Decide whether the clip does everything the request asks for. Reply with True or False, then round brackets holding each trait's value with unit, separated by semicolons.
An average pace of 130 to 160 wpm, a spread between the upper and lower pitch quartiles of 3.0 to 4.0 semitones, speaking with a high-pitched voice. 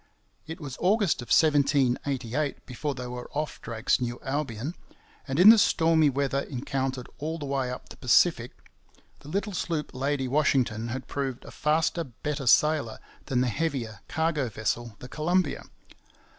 False (155 wpm; 3.7 semitones; 140 Hz)